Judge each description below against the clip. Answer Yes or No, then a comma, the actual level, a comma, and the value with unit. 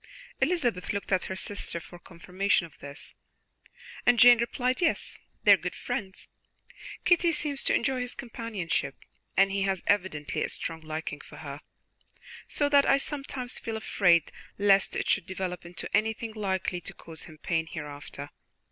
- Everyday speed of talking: Yes, average, 160 wpm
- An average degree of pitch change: No, wide, 6.1 semitones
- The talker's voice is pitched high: Yes, high, 195 Hz